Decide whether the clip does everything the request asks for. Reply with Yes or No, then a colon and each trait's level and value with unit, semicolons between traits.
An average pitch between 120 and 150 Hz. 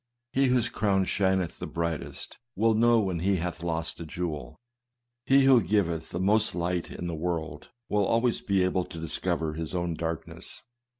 No: very low, 90 Hz